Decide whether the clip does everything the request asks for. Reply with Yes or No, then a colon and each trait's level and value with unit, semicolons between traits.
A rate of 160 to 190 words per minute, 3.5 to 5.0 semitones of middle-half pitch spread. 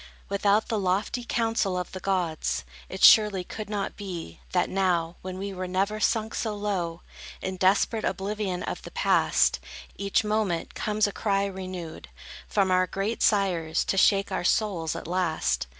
No: average, 165 wpm; narrow, 2.4 semitones